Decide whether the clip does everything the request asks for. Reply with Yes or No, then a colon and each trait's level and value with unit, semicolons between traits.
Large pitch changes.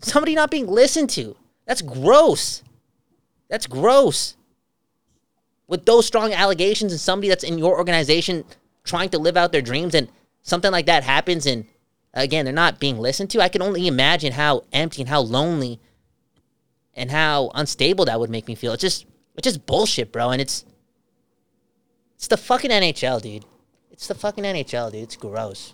Yes: wide, 7.2 semitones